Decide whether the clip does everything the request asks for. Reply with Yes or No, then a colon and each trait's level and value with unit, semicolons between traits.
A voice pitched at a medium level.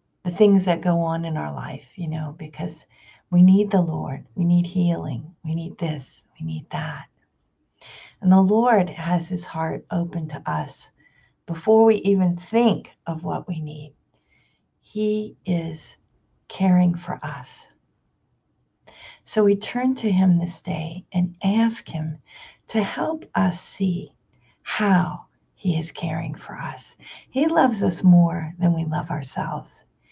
Yes: medium, 175 Hz